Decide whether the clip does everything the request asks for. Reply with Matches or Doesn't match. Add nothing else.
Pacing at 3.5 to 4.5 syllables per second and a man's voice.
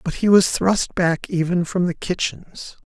Matches